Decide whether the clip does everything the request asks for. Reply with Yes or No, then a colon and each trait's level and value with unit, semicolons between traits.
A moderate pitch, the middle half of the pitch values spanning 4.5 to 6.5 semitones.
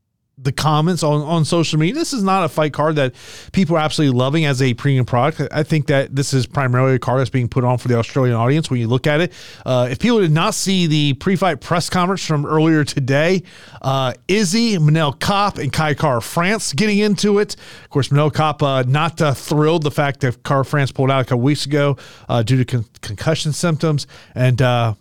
No: medium, 150 Hz; average, 3.9 semitones